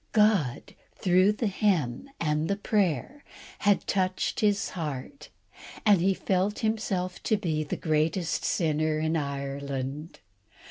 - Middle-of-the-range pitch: Yes, medium, 180 Hz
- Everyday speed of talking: No, slow, 125 wpm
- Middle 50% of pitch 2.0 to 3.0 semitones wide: No, average, 5.0 semitones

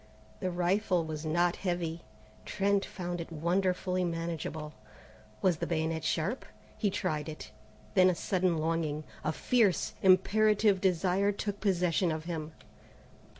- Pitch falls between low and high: Yes, medium, 175 Hz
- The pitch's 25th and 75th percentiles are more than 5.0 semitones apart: No, average, 2.9 semitones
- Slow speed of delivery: Yes, slow, 130 wpm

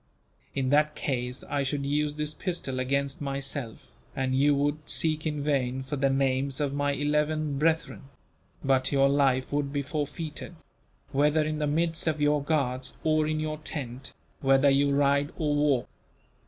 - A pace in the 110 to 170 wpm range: Yes, average, 165 wpm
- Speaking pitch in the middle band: Yes, medium, 145 Hz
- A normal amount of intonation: No, narrow, 1.8 semitones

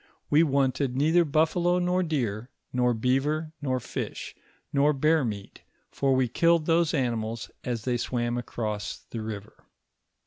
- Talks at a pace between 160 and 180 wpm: No, average, 140 wpm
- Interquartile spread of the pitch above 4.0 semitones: Yes, average, 4.7 semitones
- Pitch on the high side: No, low, 130 Hz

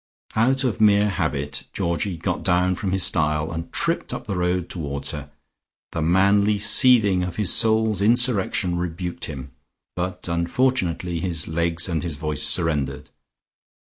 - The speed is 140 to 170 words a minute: Yes, average, 145 wpm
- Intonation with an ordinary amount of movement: Yes, average, 3.9 semitones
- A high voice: No, very low, 90 Hz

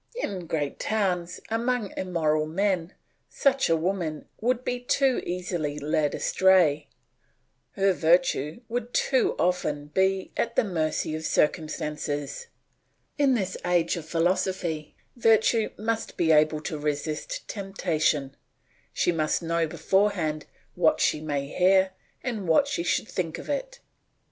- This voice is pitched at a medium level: Yes, medium, 180 Hz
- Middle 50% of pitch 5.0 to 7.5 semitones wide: Yes, average, 5.3 semitones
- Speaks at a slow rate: Yes, slow, 130 wpm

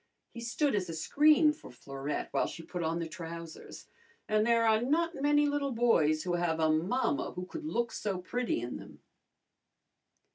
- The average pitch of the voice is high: Yes, high, 215 Hz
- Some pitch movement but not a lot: No, wide, 8.9 semitones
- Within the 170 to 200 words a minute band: Yes, average, 180 wpm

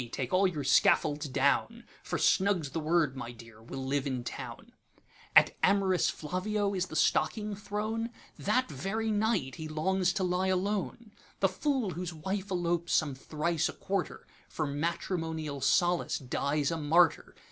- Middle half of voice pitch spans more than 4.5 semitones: Yes, average, 5.0 semitones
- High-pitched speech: No, medium, 175 Hz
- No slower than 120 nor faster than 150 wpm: Yes, average, 140 wpm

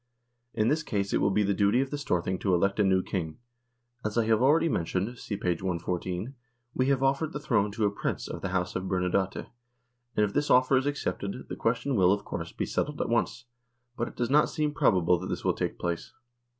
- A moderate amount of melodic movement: No, wide, 5.8 semitones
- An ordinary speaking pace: No, fast, 230 wpm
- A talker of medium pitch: No, low, 105 Hz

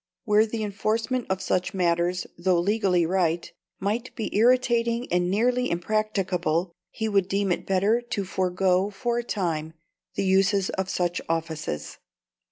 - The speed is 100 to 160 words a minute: Yes, average, 145 wpm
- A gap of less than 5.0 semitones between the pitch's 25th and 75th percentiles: Yes, average, 3.5 semitones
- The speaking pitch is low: No, high, 195 Hz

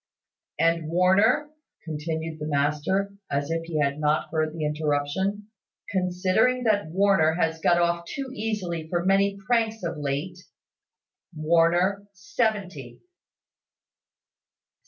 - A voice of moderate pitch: Yes, medium, 170 Hz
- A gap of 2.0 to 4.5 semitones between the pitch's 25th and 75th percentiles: Yes, average, 4.1 semitones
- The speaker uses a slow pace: Yes, slow, 115 wpm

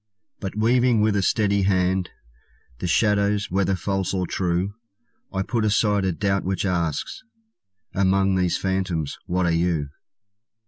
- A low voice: Yes, very low, 95 Hz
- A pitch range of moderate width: No, narrow, 2.0 semitones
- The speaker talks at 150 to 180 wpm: No, average, 140 wpm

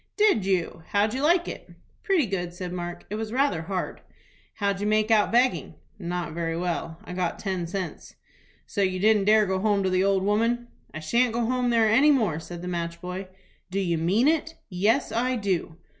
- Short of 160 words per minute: No, fast, 205 wpm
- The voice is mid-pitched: No, high, 200 Hz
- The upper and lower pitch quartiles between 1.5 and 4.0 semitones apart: No, average, 4.5 semitones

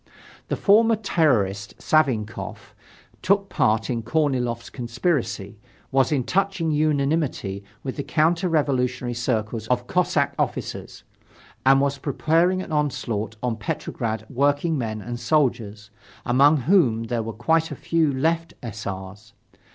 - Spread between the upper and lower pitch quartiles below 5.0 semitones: No, wide, 5.6 semitones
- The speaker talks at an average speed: No, slow, 125 wpm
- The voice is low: Yes, low, 130 Hz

